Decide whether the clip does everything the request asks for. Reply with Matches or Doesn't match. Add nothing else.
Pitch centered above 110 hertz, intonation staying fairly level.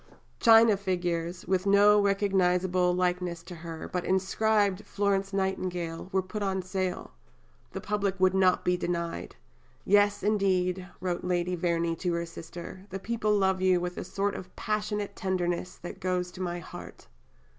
Matches